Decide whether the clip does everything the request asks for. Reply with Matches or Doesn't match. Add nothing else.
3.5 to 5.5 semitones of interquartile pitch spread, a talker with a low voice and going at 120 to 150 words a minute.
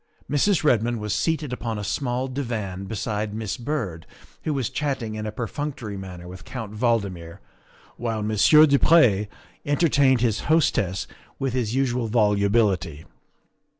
Matches